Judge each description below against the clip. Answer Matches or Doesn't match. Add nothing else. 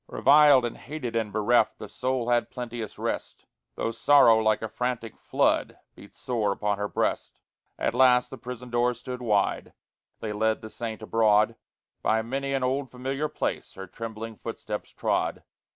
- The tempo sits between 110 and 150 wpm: Doesn't match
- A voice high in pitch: Doesn't match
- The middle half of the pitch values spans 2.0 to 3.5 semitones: Matches